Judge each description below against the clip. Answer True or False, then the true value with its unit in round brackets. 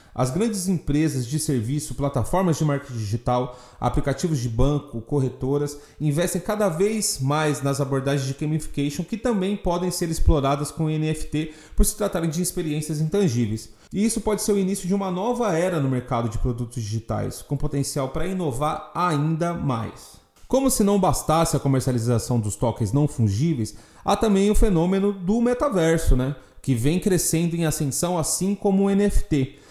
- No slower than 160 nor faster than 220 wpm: True (165 wpm)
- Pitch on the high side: False (155 Hz)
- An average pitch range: False (5.7 semitones)